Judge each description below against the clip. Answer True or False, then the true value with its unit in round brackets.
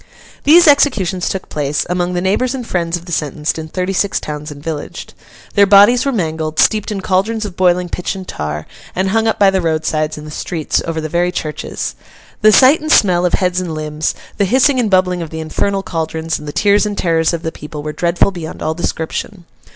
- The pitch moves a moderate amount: True (4.1 semitones)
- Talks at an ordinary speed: False (220 wpm)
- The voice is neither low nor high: True (180 Hz)